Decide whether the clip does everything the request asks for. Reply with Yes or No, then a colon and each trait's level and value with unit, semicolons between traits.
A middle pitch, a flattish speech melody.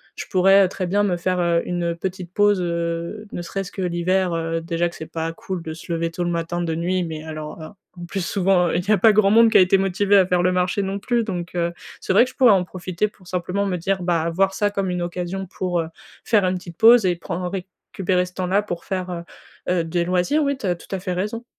Yes: medium, 180 Hz; narrow, 2.2 semitones